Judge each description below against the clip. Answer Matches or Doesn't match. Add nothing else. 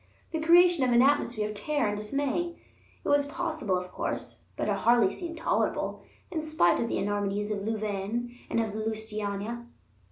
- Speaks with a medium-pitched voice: Doesn't match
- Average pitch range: Doesn't match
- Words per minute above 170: Matches